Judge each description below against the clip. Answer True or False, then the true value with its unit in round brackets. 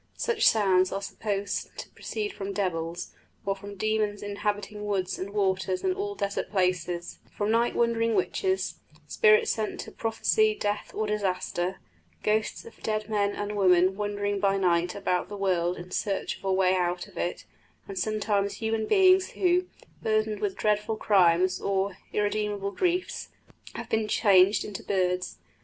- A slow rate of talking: False (155 wpm)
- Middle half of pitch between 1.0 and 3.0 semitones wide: True (2.4 semitones)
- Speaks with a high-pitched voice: True (205 Hz)